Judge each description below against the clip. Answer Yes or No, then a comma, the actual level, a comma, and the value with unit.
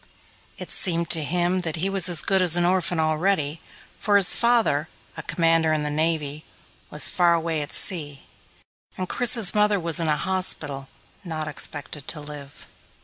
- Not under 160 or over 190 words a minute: Yes, average, 170 wpm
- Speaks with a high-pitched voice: No, medium, 165 Hz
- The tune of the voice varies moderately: Yes, average, 3.4 semitones